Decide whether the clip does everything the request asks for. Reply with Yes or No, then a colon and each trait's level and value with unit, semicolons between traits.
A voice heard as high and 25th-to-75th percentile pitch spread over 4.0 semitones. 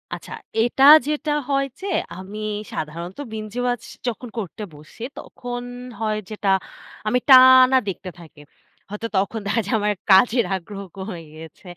Yes: high, 215 Hz; average, 4.5 semitones